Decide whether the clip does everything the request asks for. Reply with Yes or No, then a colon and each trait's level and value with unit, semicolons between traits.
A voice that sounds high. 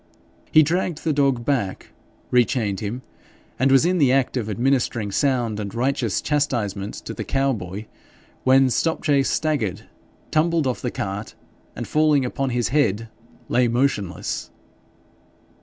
No: low, 130 Hz